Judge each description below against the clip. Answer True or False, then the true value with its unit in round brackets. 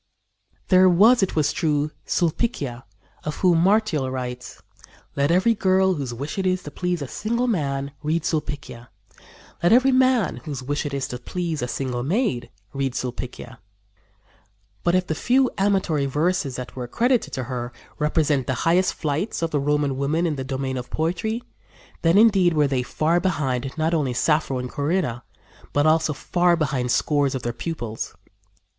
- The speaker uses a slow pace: False (170 wpm)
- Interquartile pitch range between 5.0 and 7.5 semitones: True (5.3 semitones)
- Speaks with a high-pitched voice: False (150 Hz)